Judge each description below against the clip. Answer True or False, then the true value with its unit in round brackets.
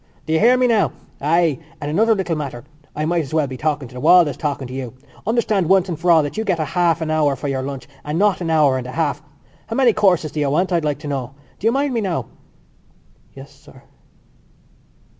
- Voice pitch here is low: False (155 Hz)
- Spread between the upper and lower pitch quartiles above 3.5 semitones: True (4.8 semitones)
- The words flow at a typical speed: False (240 wpm)